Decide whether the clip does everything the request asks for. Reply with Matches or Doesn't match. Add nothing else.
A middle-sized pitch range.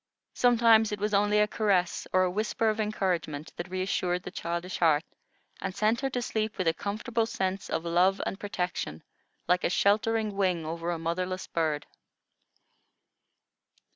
Matches